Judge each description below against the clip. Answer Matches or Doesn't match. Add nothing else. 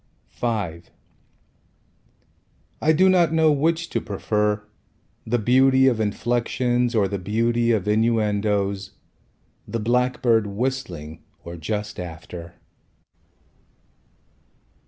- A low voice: Matches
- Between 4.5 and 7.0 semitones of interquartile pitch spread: Doesn't match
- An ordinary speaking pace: Doesn't match